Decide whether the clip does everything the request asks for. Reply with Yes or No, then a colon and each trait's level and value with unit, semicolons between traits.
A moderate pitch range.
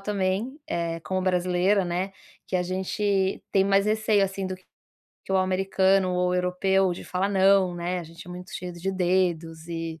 No: narrow, 1.5 semitones